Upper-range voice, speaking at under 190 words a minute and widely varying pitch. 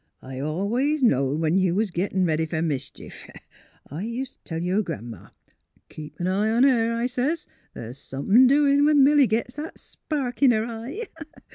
No: high, 215 Hz; average, 195 wpm; wide, 8.4 semitones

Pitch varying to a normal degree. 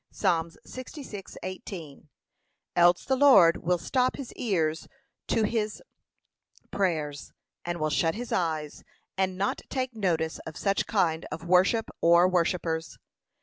Yes: average, 4.6 semitones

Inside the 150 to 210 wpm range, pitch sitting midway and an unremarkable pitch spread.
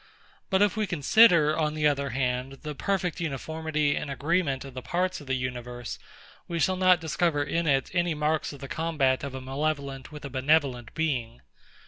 Yes: average, 185 wpm; medium, 150 Hz; average, 3.6 semitones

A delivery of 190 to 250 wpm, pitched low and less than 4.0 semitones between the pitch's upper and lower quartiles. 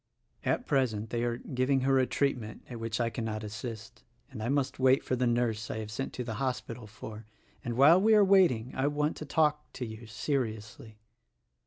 Yes: average, 200 wpm; low, 120 Hz; average, 3.6 semitones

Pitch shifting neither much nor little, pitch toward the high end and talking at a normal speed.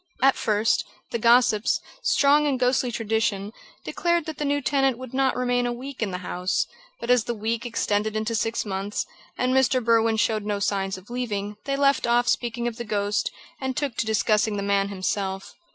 Yes: average, 3.5 semitones; high, 230 Hz; average, 195 wpm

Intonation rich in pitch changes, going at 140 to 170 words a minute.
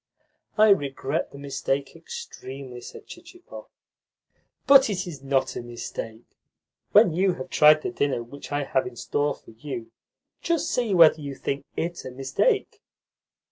Yes: wide, 6.7 semitones; average, 150 wpm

